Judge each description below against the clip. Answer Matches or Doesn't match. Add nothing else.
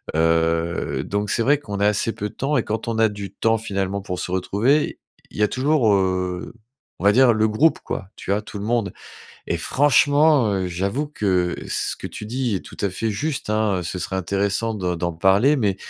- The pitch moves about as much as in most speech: Matches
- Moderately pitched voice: Doesn't match